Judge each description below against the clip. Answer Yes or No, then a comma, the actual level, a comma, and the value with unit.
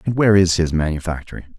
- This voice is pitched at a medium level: No, very low, 85 Hz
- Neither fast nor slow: Yes, average, 190 wpm